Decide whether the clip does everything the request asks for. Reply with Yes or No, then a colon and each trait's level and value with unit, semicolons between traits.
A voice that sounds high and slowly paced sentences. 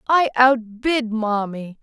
Yes: high, 235 Hz; slow, 100 wpm